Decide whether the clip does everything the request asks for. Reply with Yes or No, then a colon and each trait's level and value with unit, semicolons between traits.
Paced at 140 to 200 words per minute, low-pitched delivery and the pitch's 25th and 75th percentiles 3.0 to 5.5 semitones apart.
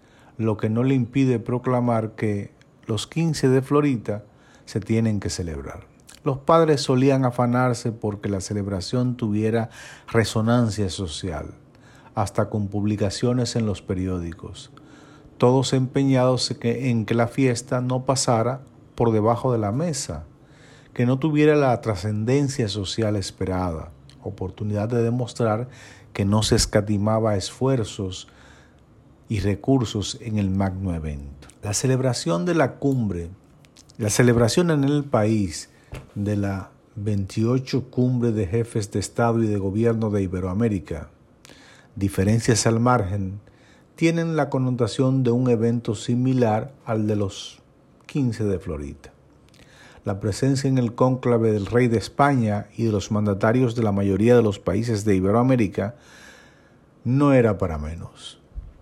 No: average, 130 wpm; low, 115 Hz; average, 3.9 semitones